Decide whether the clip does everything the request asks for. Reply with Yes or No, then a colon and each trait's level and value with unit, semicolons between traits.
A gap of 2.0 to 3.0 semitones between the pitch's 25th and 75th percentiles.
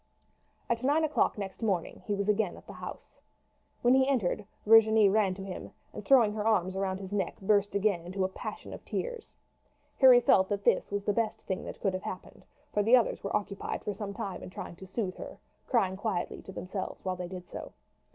Yes: average, 2.7 semitones